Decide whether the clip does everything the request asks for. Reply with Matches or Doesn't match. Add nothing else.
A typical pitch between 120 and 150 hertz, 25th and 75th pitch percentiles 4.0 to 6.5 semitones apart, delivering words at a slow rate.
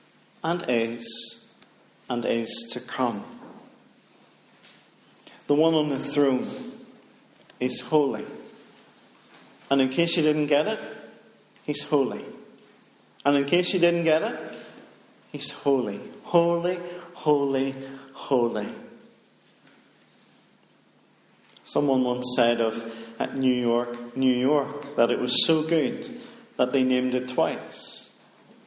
Matches